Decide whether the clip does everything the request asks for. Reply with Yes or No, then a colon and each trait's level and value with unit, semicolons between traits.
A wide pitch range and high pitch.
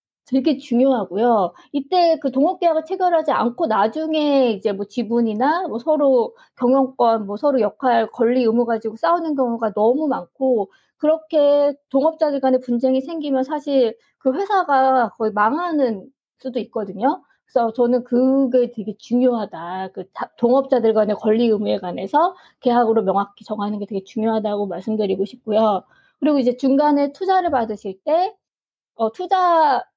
No: average, 4.8 semitones; very high, 255 Hz